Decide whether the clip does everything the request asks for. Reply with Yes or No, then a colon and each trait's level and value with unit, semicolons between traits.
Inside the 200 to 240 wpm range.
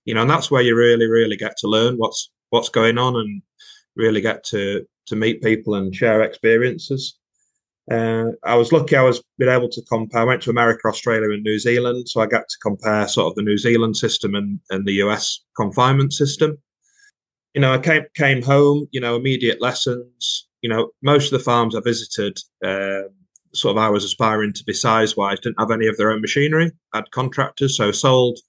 Yes: fast, 205 wpm